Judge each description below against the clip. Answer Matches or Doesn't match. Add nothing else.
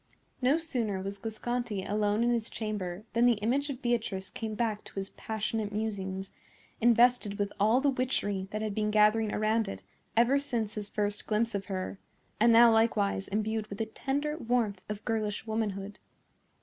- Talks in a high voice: Matches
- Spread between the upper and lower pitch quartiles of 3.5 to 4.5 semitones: Doesn't match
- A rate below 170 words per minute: Doesn't match